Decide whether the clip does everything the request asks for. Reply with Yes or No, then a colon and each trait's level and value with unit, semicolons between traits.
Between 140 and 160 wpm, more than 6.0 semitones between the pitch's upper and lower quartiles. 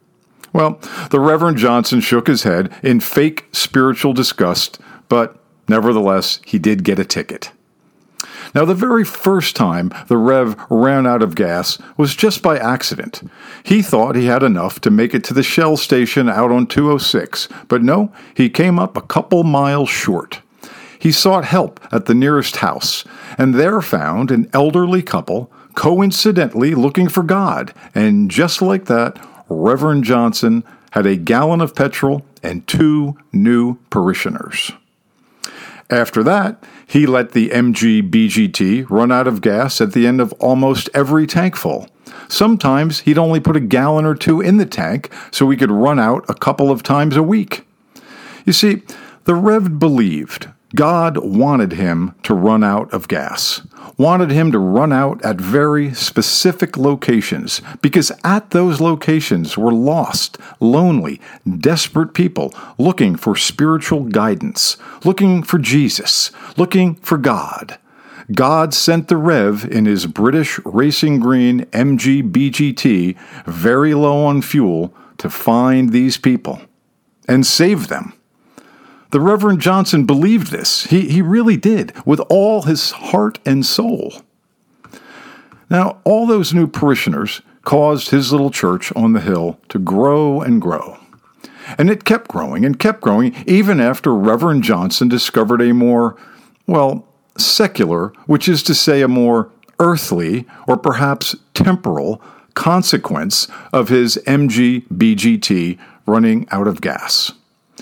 Yes: average, 145 wpm; wide, 7.1 semitones